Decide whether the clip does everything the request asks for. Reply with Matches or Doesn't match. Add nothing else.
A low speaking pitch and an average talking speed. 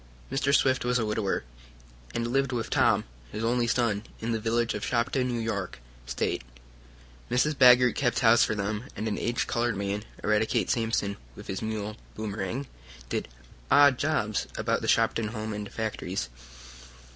Matches